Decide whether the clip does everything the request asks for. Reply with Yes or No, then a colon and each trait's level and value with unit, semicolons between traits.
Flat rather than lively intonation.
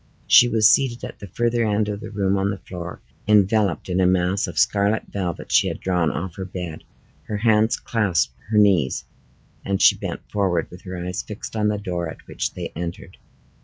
No: average, 3.0 semitones